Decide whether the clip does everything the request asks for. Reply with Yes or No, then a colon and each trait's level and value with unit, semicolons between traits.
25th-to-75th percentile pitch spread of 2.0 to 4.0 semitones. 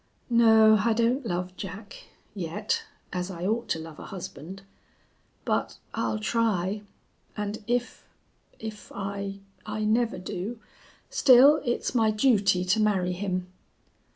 Yes: average, 3.5 semitones